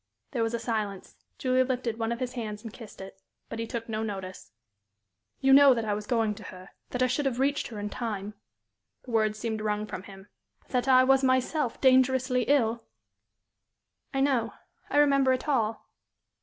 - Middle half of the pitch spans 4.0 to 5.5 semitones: No, average, 3.2 semitones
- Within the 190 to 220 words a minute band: Yes, average, 195 wpm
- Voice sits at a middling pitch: No, high, 235 Hz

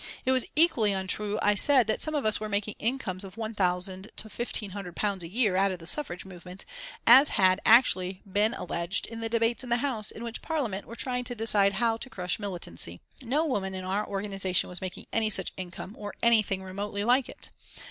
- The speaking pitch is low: No, high, 205 Hz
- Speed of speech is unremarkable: No, fast, 210 wpm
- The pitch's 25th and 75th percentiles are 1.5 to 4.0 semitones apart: Yes, average, 3.7 semitones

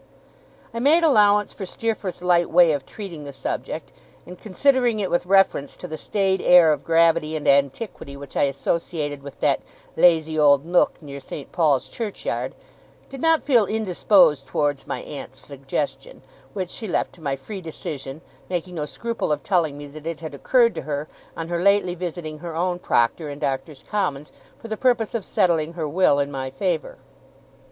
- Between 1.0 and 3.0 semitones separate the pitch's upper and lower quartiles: No, average, 5.2 semitones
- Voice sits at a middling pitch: Yes, medium, 170 Hz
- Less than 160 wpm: No, average, 180 wpm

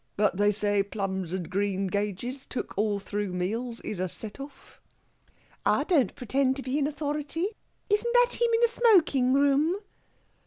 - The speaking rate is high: No, average, 160 wpm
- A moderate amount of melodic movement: No, wide, 6.6 semitones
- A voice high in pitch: Yes, very high, 250 Hz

